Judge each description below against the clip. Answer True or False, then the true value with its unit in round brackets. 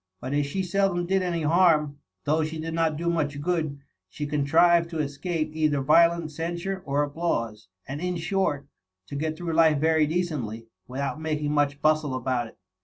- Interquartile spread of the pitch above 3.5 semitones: False (2.9 semitones)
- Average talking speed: True (180 wpm)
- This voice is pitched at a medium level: True (155 Hz)